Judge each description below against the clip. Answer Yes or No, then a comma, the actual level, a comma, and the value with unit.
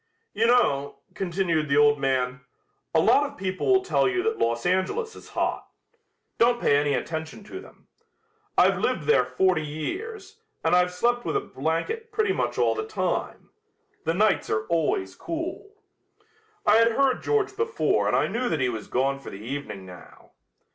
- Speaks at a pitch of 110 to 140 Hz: No, high, 190 Hz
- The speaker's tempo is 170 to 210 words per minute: Yes, average, 175 wpm